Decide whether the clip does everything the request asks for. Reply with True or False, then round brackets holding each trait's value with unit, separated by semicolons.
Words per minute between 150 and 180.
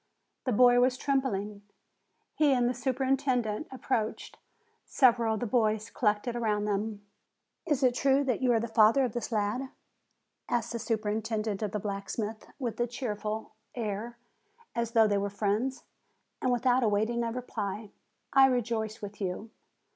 True (155 wpm)